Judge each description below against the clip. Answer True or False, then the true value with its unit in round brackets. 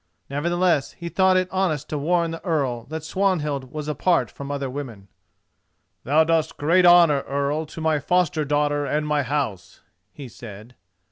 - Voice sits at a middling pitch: True (150 Hz)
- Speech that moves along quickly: False (160 wpm)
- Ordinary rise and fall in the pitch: True (3.3 semitones)